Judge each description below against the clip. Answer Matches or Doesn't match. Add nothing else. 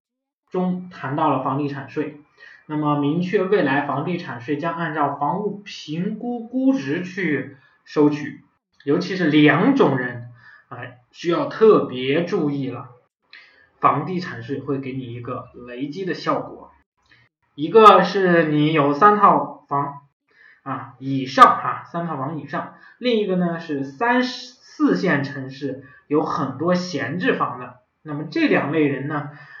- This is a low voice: Doesn't match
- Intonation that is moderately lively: Matches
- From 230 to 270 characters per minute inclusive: Doesn't match